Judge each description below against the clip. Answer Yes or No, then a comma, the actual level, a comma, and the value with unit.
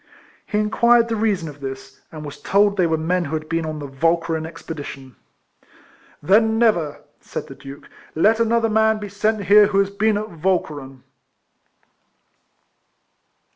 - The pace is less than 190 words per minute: Yes, average, 155 wpm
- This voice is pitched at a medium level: Yes, medium, 180 Hz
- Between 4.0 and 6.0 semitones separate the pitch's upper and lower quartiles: Yes, wide, 5.5 semitones